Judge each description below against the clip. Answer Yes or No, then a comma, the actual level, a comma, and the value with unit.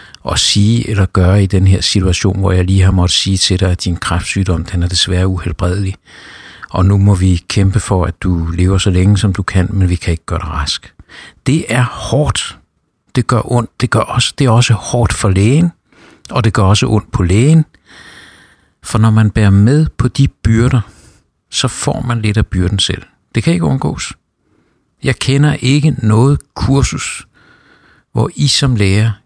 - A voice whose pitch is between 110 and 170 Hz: No, low, 100 Hz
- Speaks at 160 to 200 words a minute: Yes, average, 195 wpm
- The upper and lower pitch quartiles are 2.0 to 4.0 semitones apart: No, average, 4.5 semitones